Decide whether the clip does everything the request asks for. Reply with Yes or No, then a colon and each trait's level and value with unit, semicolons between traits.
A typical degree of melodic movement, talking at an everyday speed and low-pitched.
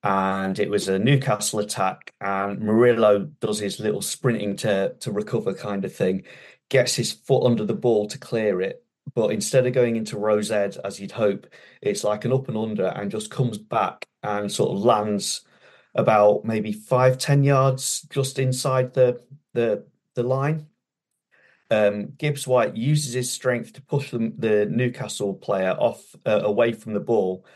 Yes: average, 4.0 semitones; average, 170 wpm; low, 115 Hz